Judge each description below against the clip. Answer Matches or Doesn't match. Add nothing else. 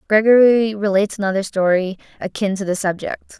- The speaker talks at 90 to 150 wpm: Matches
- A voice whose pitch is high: Matches